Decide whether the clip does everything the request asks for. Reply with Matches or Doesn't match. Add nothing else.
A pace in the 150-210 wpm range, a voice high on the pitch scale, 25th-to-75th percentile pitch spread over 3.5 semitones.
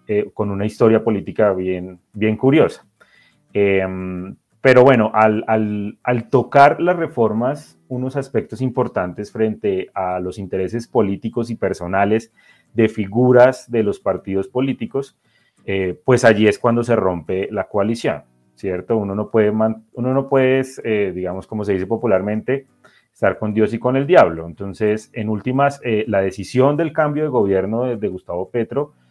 Doesn't match